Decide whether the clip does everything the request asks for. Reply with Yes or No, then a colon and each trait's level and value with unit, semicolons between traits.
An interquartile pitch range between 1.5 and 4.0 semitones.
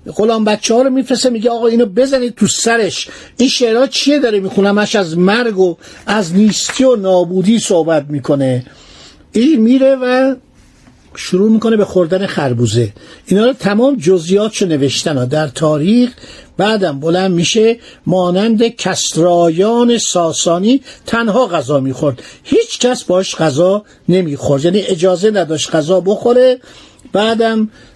No: average, 5.3 semitones